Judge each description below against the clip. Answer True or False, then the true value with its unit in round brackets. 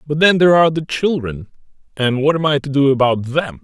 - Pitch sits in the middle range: True (145 Hz)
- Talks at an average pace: False (230 wpm)